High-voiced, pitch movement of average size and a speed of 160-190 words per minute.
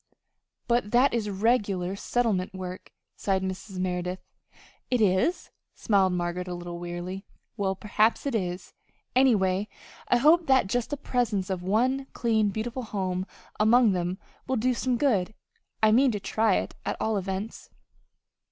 No: high, 205 Hz; average, 4.4 semitones; average, 150 wpm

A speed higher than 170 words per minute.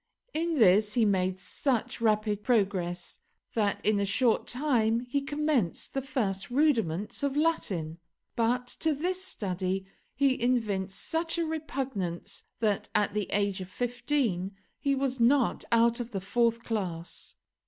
No: average, 145 wpm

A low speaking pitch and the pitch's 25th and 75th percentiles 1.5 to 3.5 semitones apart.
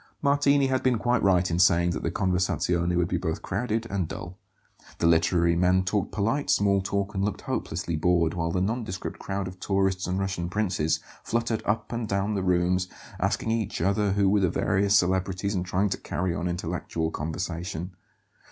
Yes: very low, 95 Hz; narrow, 2.6 semitones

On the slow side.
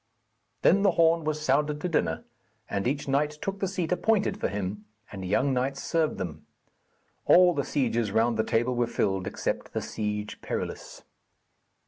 No: average, 165 wpm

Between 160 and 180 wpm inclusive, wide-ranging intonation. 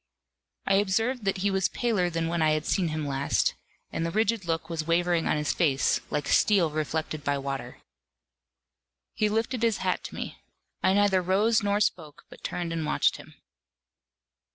No: average, 175 wpm; average, 4.6 semitones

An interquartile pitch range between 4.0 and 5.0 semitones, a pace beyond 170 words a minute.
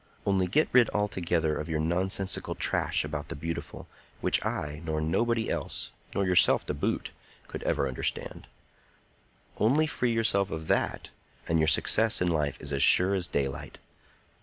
No: average, 4.6 semitones; average, 155 wpm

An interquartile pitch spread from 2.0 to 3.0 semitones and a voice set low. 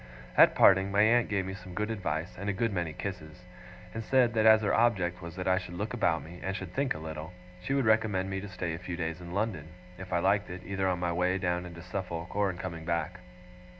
Yes: average, 2.7 semitones; very low, 95 Hz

